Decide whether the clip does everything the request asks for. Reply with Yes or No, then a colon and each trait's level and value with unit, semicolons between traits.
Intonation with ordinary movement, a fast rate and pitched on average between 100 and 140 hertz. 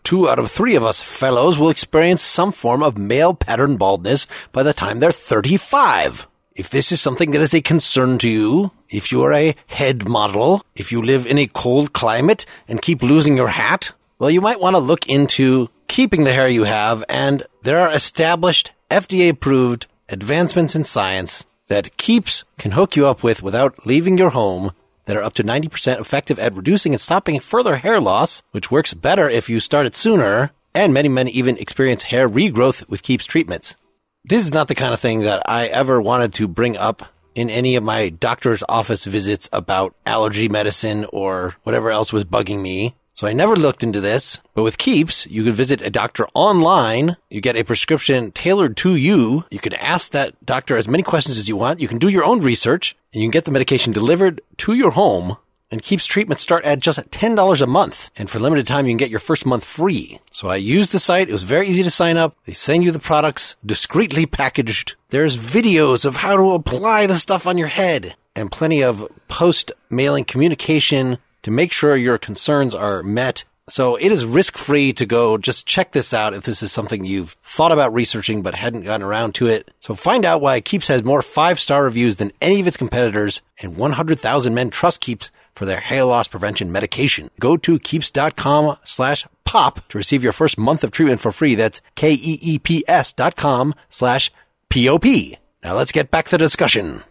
No: wide, 6.3 semitones; fast, 210 wpm; low, 135 Hz